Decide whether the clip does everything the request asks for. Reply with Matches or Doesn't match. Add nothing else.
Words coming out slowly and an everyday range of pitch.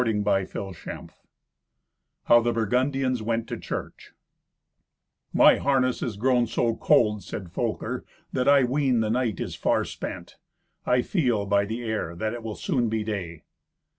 Doesn't match